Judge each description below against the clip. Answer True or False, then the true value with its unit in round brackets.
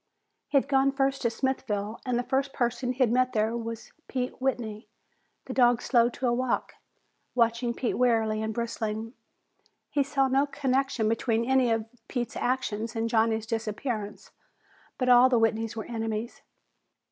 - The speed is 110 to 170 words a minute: True (155 wpm)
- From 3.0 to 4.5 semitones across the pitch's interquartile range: False (2.5 semitones)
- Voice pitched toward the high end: True (235 Hz)